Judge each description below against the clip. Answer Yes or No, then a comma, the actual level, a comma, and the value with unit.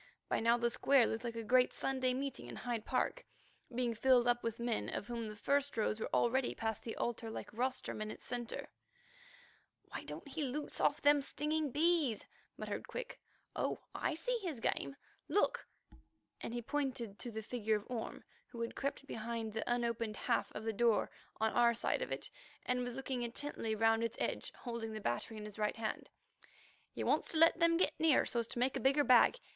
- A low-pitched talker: No, high, 240 Hz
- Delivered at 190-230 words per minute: Yes, fast, 205 wpm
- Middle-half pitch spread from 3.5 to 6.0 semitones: No, average, 3.1 semitones